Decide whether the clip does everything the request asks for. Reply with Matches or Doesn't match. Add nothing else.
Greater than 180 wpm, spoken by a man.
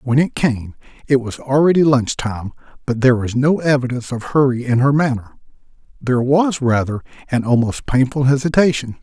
Doesn't match